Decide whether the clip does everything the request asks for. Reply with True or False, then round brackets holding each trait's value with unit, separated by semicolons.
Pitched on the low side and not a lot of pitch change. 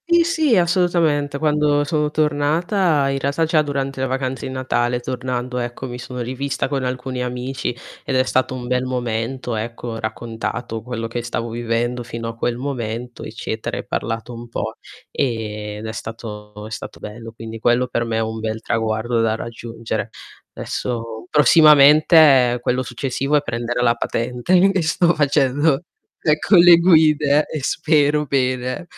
False (125 Hz; 3.9 semitones)